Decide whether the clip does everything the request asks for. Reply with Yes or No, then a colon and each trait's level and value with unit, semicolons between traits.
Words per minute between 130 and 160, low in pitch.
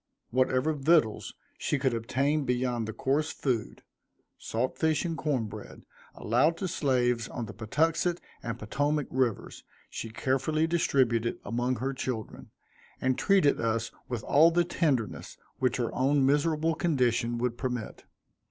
Yes: average, 140 wpm; low, 130 Hz